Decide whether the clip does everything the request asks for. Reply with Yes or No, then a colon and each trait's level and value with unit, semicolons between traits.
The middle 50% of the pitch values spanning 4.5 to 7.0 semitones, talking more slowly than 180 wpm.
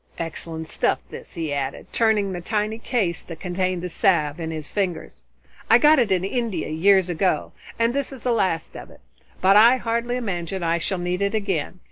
No: average, 4.8 semitones; average, 195 wpm